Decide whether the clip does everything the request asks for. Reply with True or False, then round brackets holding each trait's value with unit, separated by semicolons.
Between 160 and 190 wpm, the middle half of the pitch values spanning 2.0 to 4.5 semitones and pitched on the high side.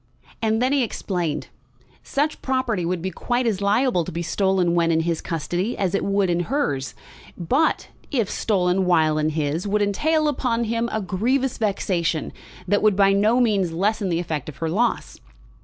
False (180 wpm; 5.2 semitones; 195 Hz)